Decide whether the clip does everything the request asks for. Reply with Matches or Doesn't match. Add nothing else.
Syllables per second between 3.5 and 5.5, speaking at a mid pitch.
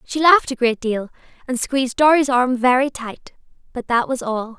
Doesn't match